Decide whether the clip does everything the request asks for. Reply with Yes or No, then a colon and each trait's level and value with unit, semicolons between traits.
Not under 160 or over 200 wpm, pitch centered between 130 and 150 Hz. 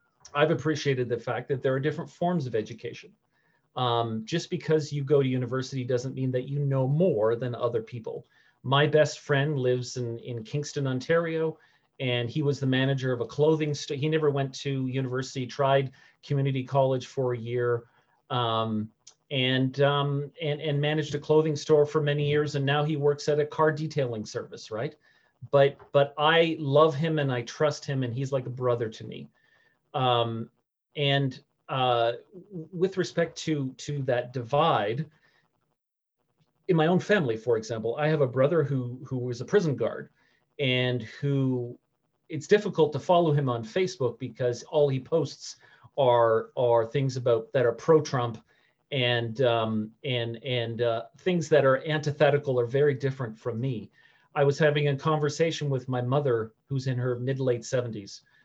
Yes: average, 170 wpm; low, 135 Hz